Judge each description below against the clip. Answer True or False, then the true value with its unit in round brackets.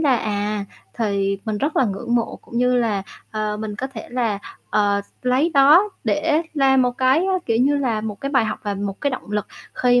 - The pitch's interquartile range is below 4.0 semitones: False (4.3 semitones)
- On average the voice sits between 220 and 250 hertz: True (235 Hz)